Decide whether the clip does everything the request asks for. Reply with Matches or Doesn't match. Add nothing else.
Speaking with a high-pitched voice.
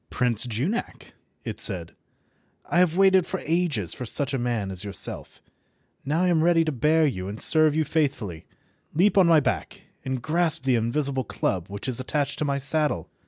Doesn't match